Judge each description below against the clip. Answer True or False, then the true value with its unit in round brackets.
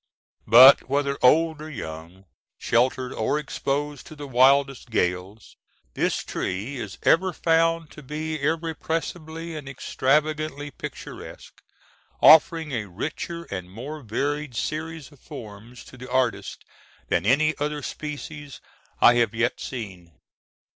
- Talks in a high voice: False (140 Hz)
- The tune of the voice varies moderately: True (4.8 semitones)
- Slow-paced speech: True (125 wpm)